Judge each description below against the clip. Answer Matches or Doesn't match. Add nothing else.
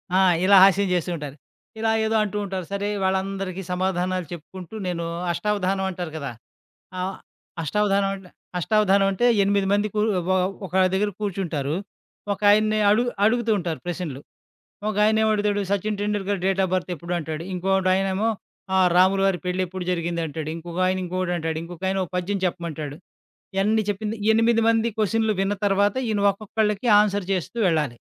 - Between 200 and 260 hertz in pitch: Doesn't match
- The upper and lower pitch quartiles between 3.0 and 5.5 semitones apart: Doesn't match